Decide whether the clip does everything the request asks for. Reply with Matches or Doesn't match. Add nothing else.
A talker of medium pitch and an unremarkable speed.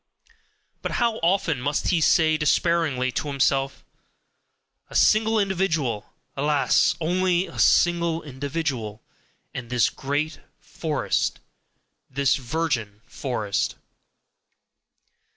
Doesn't match